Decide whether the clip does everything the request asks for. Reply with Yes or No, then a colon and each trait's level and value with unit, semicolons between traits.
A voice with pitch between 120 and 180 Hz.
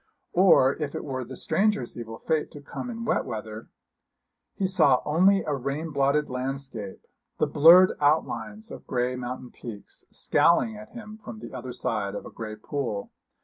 Yes: medium, 140 Hz